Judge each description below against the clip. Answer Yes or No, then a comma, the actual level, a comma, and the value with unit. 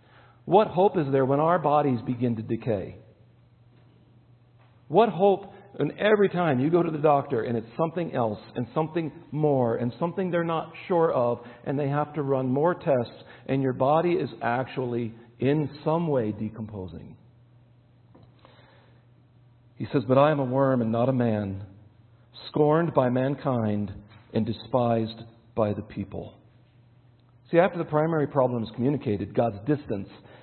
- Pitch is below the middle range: Yes, low, 125 Hz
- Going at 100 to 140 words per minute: No, average, 150 wpm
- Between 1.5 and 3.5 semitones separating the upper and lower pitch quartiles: No, average, 4.2 semitones